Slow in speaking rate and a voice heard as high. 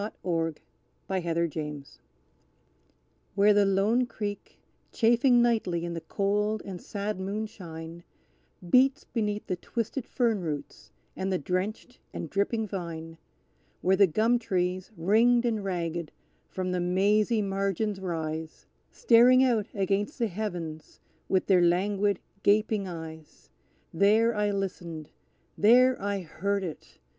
Yes: slow, 130 wpm; high, 195 Hz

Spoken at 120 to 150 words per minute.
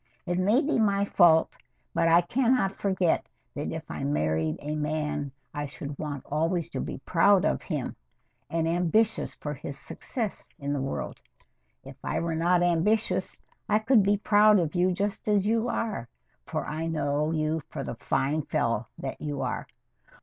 No: average, 175 wpm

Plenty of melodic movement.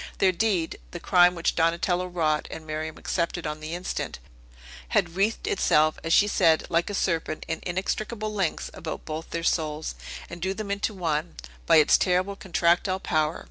No: average, 3.0 semitones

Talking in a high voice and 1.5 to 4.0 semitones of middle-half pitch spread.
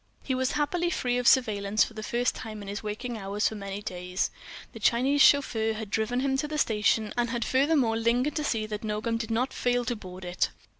Yes: high, 230 Hz; average, 3.4 semitones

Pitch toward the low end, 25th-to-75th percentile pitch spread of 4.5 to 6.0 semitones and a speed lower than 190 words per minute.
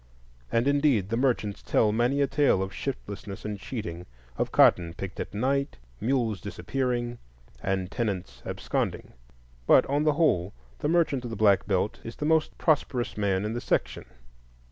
Yes: low, 115 Hz; wide, 5.4 semitones; average, 165 wpm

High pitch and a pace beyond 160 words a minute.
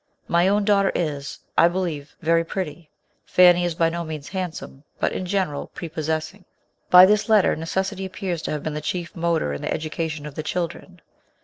No: medium, 170 Hz; average, 190 wpm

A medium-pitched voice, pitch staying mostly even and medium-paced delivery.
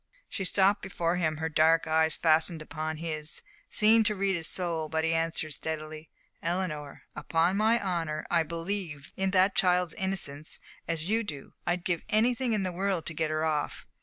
No: medium, 165 Hz; average, 3.3 semitones; average, 180 wpm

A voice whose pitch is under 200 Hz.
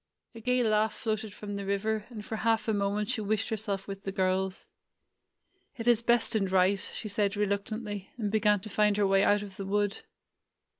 No: high, 210 Hz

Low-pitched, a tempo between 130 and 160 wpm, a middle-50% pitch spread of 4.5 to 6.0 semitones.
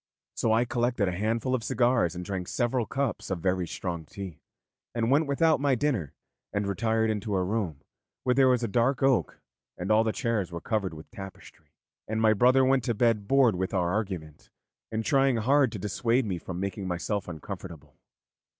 No: low, 110 Hz; average, 185 wpm; average, 4.8 semitones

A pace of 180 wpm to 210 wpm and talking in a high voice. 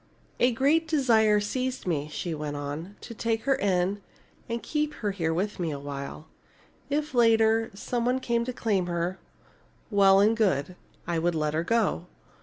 No: average, 170 wpm; high, 205 Hz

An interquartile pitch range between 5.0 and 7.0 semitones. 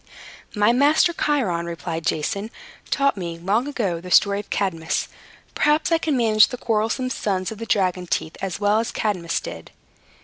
Yes: average, 5.3 semitones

